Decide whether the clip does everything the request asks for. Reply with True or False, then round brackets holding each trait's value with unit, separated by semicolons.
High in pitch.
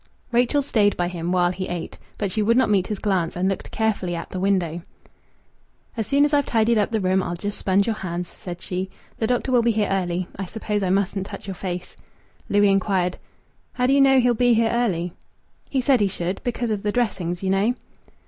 True (200 Hz)